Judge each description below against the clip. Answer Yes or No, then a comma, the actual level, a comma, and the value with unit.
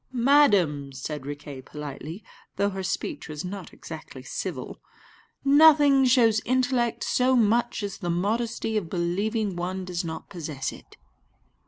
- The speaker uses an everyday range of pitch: No, wide, 6.6 semitones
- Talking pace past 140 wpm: No, slow, 135 wpm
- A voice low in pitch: No, high, 195 Hz